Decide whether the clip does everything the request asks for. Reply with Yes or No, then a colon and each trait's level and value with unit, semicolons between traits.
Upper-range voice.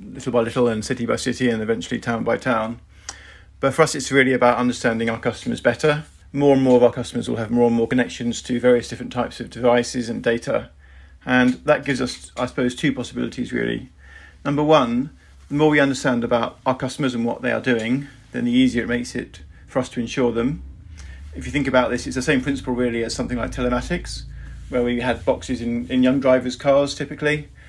No: low, 125 Hz